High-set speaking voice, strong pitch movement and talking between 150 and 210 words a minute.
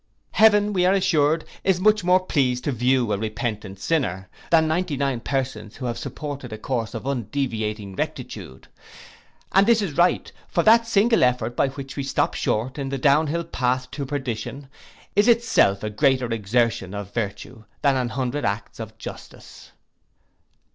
No: low, 135 Hz; wide, 6.2 semitones; average, 165 wpm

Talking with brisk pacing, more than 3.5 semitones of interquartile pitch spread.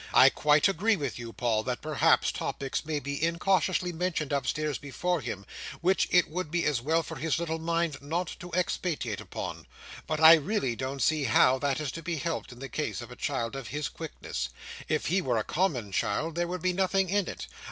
Yes: fast, 210 wpm; average, 4.3 semitones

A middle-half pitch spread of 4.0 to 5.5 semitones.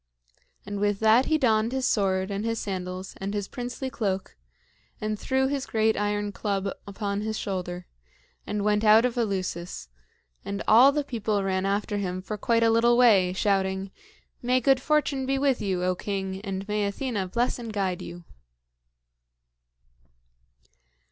No: average, 3.5 semitones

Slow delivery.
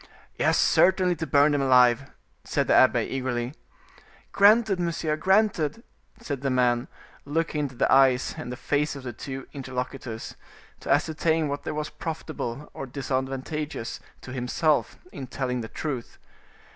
No: average, 145 wpm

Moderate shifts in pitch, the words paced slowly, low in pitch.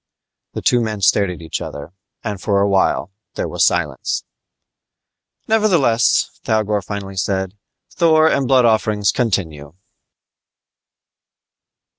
Yes: average, 4.0 semitones; slow, 110 wpm; low, 105 Hz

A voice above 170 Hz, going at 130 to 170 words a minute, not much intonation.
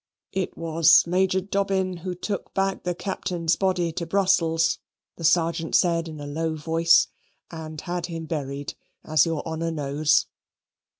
No: medium, 165 Hz; average, 145 wpm; narrow, 2.3 semitones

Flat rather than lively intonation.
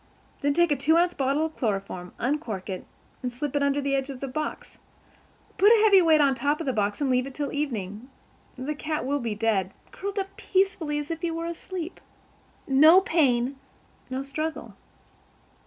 No: average, 4.2 semitones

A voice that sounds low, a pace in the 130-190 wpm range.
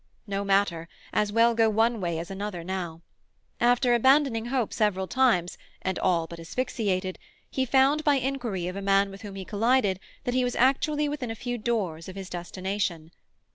No: high, 205 Hz; average, 180 wpm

